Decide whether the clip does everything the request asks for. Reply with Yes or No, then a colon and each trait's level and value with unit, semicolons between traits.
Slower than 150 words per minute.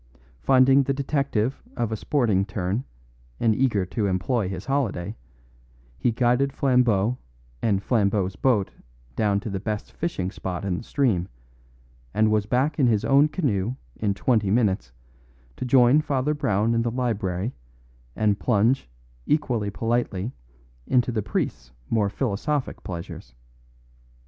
Yes: slow, 135 wpm